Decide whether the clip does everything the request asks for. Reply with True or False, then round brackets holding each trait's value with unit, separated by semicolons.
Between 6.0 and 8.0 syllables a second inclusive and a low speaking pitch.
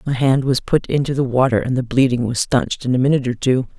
True (6.4 syllables/s; 125 Hz)